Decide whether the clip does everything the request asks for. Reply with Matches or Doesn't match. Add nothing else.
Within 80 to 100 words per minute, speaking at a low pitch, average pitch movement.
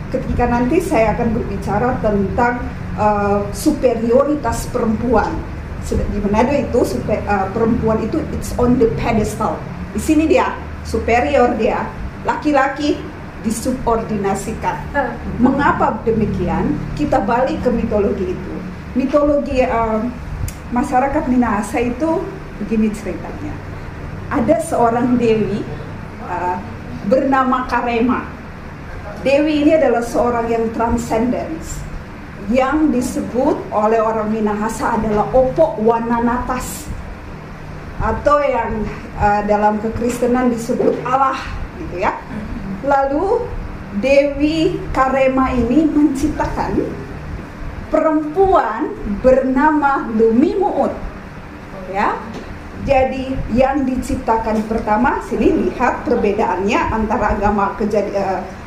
Doesn't match